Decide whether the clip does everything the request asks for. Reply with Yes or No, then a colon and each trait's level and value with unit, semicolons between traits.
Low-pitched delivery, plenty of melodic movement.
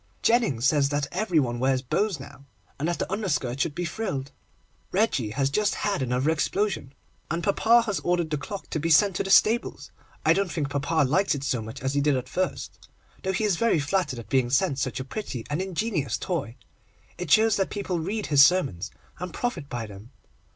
No: medium, 155 Hz; wide, 6.4 semitones